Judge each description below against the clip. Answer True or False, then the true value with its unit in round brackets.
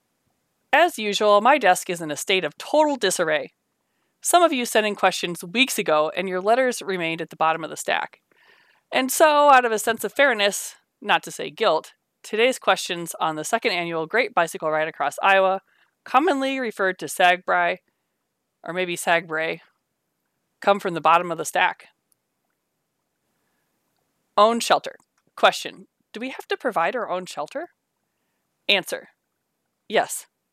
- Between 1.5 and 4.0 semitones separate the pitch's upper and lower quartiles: False (5.4 semitones)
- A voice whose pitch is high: True (195 Hz)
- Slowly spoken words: False (155 wpm)